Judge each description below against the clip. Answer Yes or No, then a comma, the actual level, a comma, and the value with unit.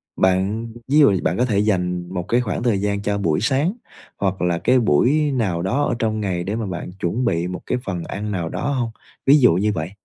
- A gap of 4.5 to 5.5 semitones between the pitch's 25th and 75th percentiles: Yes, average, 5.2 semitones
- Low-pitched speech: Yes, low, 100 Hz